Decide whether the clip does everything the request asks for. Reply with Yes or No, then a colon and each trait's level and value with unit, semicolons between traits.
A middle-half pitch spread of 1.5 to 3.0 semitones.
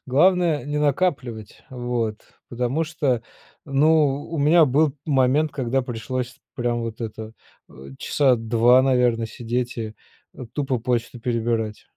No: average, 3.8 semitones